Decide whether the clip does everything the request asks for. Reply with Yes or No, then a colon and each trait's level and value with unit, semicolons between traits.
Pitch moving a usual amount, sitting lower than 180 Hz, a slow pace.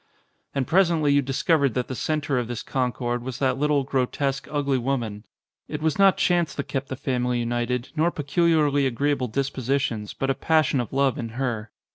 No: average, 3.0 semitones; low, 135 Hz; average, 190 wpm